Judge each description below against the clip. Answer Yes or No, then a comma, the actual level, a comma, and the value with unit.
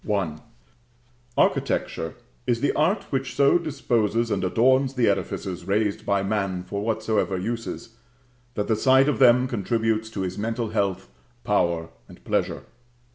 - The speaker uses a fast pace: No, slow, 135 wpm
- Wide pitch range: No, average, 4.2 semitones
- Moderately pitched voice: No, low, 110 Hz